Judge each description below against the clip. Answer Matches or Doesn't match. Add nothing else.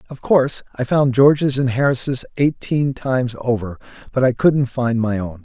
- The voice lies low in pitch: Matches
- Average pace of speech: Matches